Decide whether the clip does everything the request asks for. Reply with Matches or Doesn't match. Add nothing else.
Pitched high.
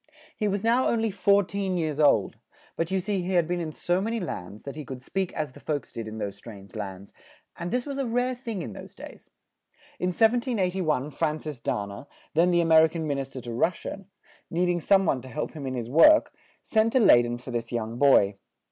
Doesn't match